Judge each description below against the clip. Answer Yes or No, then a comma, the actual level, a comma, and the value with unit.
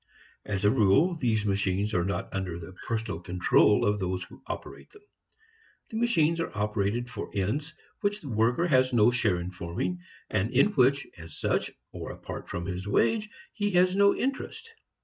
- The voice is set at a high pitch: No, low, 110 Hz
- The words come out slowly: No, average, 175 wpm